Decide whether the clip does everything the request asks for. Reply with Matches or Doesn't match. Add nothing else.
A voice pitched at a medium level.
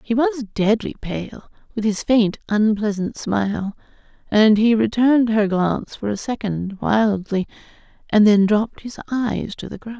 Doesn't match